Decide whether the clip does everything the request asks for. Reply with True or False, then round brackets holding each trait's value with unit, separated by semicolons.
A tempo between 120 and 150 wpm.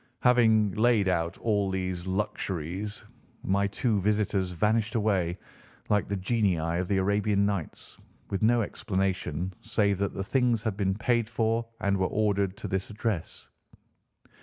True (145 wpm)